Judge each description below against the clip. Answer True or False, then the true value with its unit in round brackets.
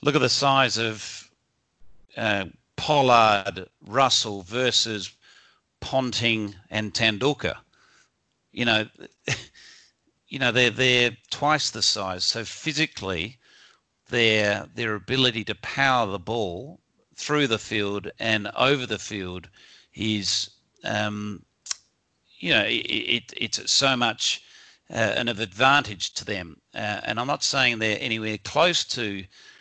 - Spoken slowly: True (120 wpm)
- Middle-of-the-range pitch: False (110 Hz)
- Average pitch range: True (3.7 semitones)